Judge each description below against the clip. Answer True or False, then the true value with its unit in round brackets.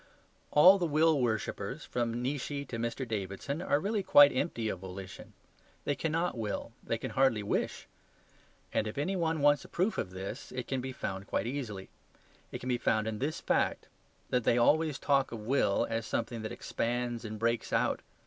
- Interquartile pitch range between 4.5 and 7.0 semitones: True (4.8 semitones)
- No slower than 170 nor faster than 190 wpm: True (185 wpm)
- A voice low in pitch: True (125 Hz)